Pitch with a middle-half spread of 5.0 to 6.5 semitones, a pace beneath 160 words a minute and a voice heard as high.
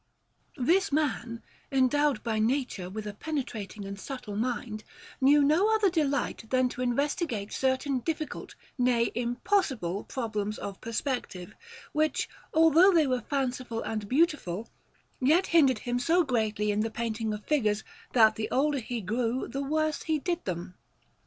Yes: average, 5.3 semitones; average, 145 wpm; very high, 250 Hz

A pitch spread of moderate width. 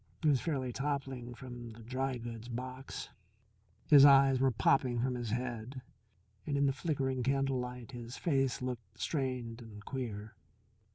No: narrow, 2.2 semitones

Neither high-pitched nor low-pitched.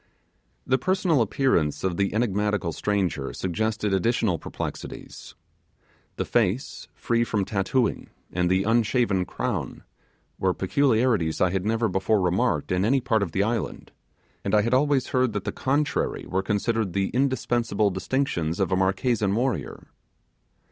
No: low, 105 Hz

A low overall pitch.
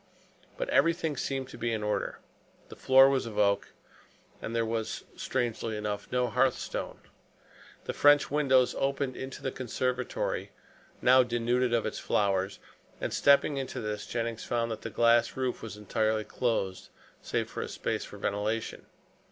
Yes: low, 120 Hz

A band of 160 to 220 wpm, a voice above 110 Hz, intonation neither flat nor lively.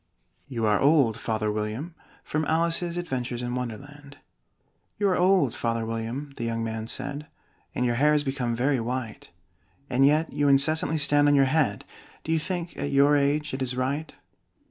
Yes: average, 175 wpm; medium, 140 Hz; average, 4.0 semitones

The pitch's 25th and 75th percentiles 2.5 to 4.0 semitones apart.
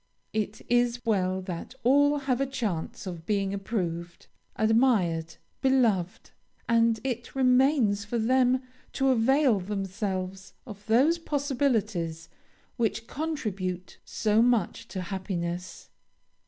No: average, 5.3 semitones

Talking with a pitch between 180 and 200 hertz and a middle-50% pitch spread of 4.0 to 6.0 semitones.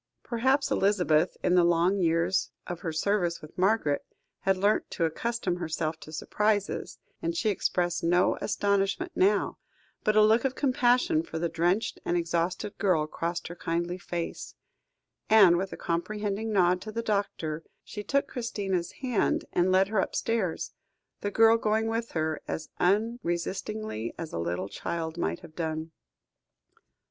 Yes: medium, 185 Hz; average, 4.3 semitones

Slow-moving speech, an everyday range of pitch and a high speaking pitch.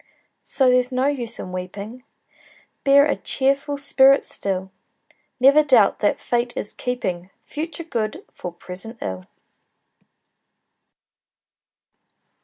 No: slow, 105 wpm; wide, 5.9 semitones; high, 245 Hz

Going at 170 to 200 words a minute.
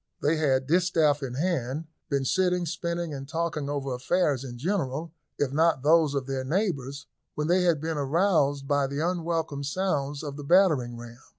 Yes: average, 175 wpm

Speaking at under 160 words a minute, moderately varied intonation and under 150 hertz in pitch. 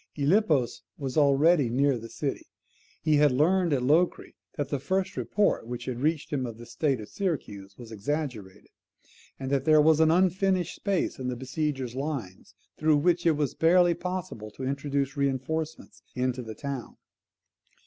No: average, 165 wpm; average, 4.2 semitones; medium, 140 Hz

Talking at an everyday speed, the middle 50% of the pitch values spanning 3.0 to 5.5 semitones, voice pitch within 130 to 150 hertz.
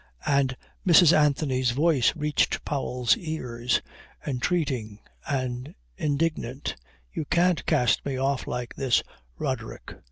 No: slow, 105 wpm; average, 3.6 semitones; medium, 140 Hz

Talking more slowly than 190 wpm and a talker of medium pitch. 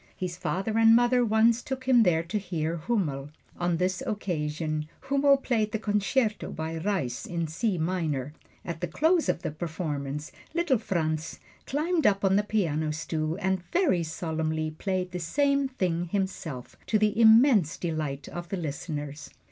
Yes: average, 160 wpm; medium, 180 Hz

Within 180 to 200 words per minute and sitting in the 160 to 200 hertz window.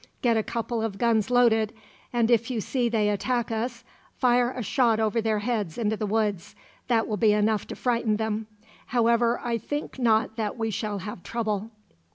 No: average, 190 wpm; high, 225 Hz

